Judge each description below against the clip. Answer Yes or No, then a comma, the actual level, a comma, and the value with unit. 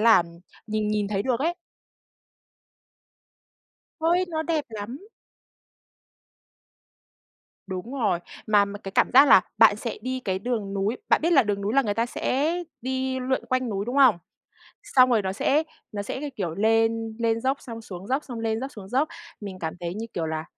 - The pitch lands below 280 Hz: Yes, high, 225 Hz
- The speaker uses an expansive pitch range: No, average, 4.5 semitones